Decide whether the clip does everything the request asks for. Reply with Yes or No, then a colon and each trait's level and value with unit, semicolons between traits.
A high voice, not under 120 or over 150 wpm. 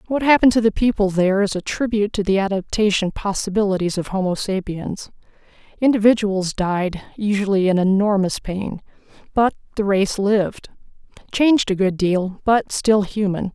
Yes: high, 200 Hz; average, 145 wpm